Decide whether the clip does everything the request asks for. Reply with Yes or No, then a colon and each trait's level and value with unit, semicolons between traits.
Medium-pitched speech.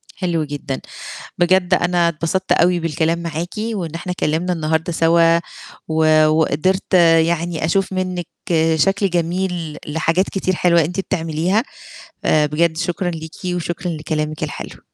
Yes: medium, 170 Hz